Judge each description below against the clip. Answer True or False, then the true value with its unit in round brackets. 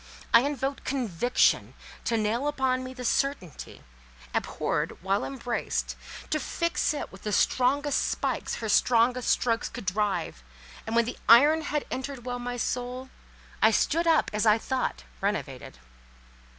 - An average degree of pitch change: True (3.3 semitones)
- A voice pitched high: True (250 Hz)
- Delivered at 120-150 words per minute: True (145 wpm)